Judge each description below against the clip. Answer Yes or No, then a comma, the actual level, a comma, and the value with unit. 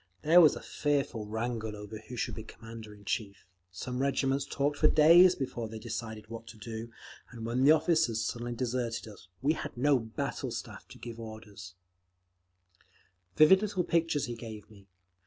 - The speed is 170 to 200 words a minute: Yes, average, 175 wpm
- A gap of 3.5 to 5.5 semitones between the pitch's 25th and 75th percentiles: Yes, average, 4.4 semitones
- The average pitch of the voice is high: No, low, 115 Hz